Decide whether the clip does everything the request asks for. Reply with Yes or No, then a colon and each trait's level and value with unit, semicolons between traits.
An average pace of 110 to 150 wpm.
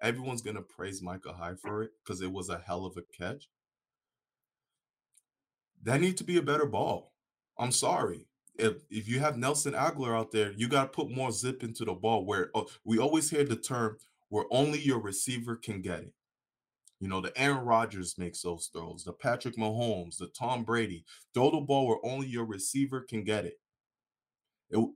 No: average, 190 wpm